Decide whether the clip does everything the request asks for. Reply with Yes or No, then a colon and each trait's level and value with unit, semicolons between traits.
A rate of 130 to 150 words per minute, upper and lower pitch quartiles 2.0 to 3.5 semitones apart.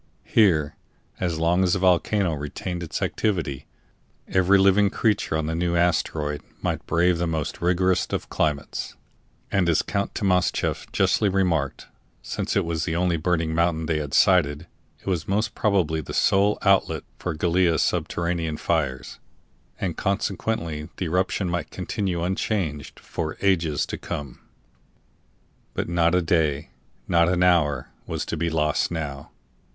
Yes: average, 145 wpm; average, 2.9 semitones